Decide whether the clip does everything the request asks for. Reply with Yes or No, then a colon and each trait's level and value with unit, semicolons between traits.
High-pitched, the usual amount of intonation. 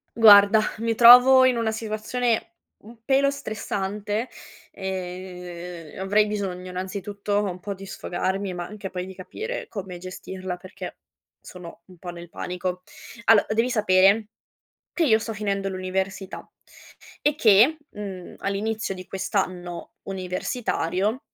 Yes: high, 195 Hz; average, 3.1 semitones